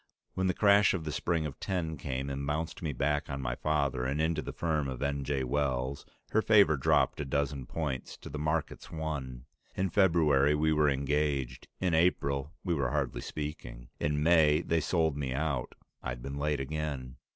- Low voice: Yes, very low, 75 Hz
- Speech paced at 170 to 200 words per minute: Yes, average, 190 wpm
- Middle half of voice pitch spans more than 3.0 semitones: No, average, 2.7 semitones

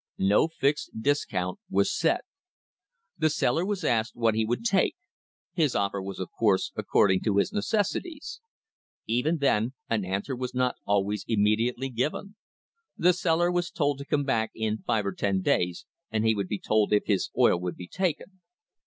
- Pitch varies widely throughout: Yes, wide, 7.5 semitones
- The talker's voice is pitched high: No, low, 115 Hz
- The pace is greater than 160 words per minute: Yes, average, 170 wpm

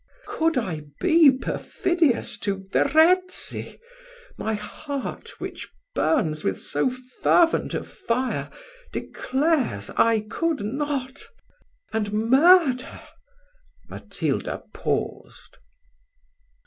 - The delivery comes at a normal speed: No, slow, 85 wpm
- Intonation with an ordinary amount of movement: No, wide, 6.6 semitones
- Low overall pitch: No, very high, 260 Hz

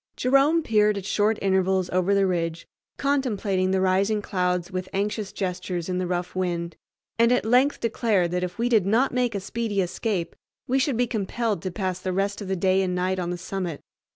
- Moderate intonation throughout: Yes, average, 3.4 semitones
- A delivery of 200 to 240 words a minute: Yes, fast, 205 wpm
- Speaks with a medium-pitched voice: No, high, 195 Hz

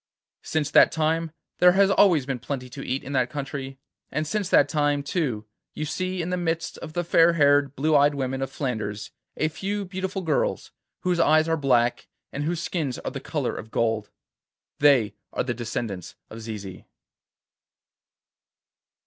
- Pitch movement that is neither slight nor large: Yes, average, 4.6 semitones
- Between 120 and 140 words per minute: No, average, 170 wpm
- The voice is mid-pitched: Yes, medium, 145 Hz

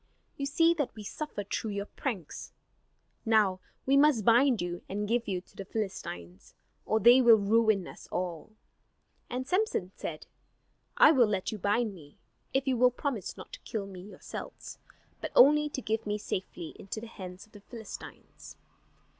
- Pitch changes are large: No, average, 4.6 semitones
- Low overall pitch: No, high, 215 Hz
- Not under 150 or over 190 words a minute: Yes, average, 170 wpm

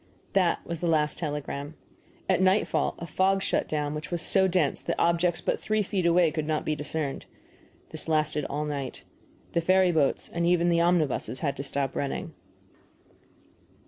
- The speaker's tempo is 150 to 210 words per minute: Yes, average, 175 wpm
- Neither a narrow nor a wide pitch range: Yes, average, 3.0 semitones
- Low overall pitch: No, medium, 165 Hz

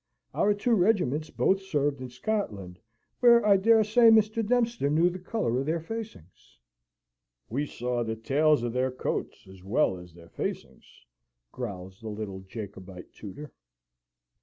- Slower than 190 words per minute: Yes, average, 150 wpm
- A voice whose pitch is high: No, medium, 140 Hz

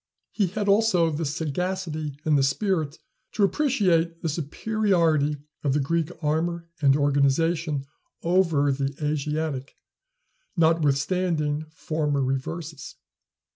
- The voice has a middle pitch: Yes, medium, 155 Hz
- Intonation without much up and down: No, average, 3.1 semitones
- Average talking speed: No, slow, 105 wpm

